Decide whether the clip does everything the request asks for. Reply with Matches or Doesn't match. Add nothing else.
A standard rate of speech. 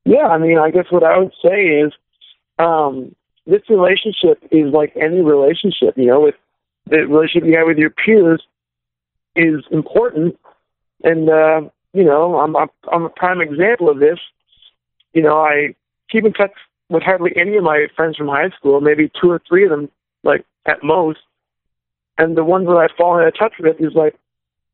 Matches